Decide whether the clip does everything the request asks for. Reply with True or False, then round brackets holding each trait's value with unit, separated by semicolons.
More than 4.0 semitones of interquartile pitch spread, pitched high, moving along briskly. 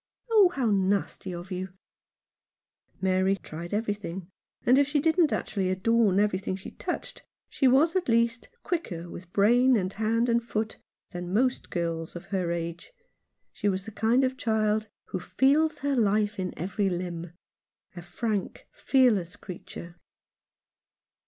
False (4.8 semitones; 205 Hz; 155 wpm)